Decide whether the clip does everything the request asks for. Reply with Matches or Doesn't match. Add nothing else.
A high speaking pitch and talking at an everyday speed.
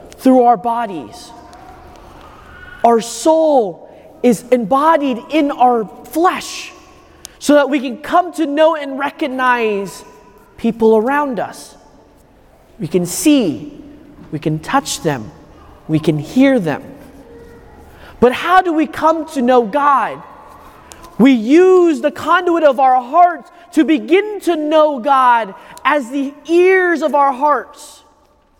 Doesn't match